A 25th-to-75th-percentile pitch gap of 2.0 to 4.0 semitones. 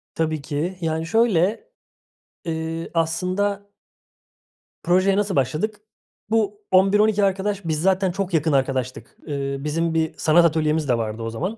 No: average, 4.4 semitones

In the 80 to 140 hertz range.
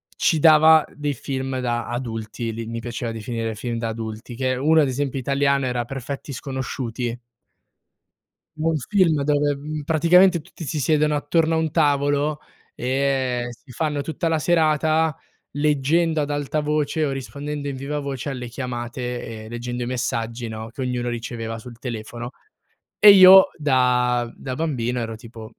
Yes: low, 135 Hz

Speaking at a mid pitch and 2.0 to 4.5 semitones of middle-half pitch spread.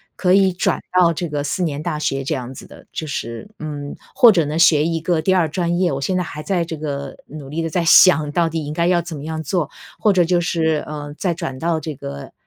Yes: medium, 160 Hz; average, 3.0 semitones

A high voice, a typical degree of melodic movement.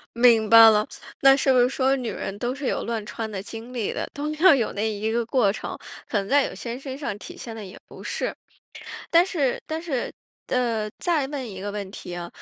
Yes: high, 235 Hz; average, 4.2 semitones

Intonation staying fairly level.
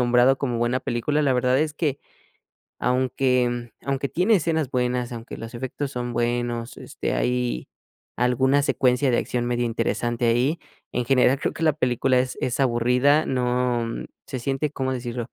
Yes: narrow, 2.0 semitones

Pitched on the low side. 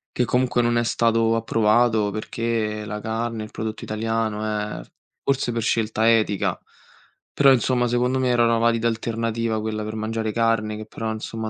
Yes: low, 115 Hz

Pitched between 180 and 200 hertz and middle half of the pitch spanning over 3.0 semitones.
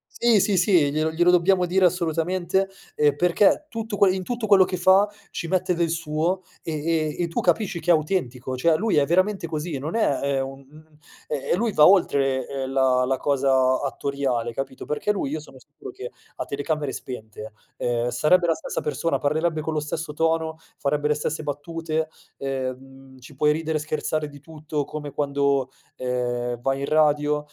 No: medium, 155 Hz; average, 3.8 semitones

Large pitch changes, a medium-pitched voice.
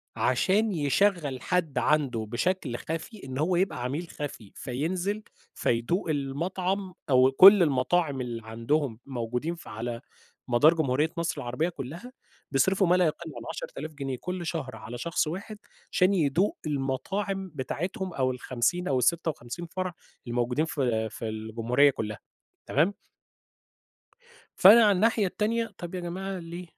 Yes: wide, 6.3 semitones; medium, 155 Hz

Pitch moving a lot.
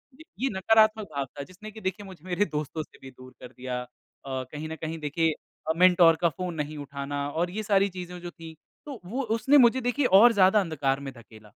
Yes: wide, 6.2 semitones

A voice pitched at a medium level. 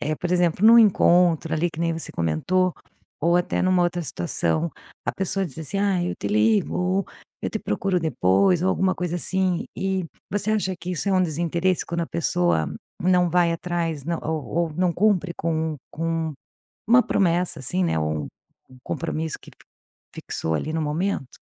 Yes: medium, 170 Hz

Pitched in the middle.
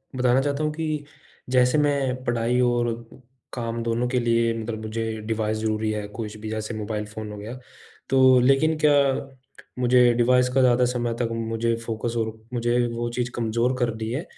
No: low, 120 Hz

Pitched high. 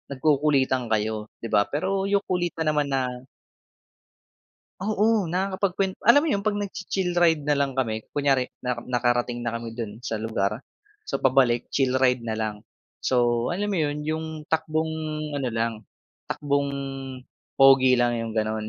No: low, 135 Hz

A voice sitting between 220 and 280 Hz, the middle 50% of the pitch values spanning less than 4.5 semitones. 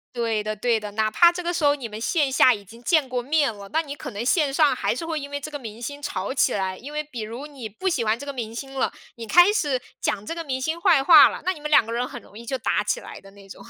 No: very high, 260 Hz; average, 5.3 semitones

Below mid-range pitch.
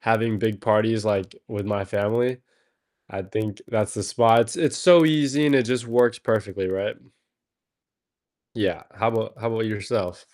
Yes: low, 110 Hz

